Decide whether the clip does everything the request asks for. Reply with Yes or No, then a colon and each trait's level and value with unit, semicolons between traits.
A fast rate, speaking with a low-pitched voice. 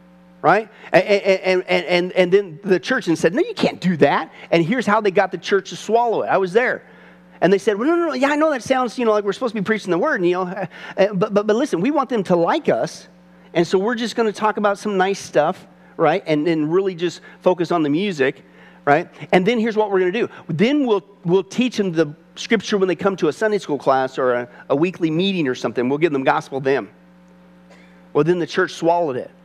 No: fast, 255 wpm; medium, 185 Hz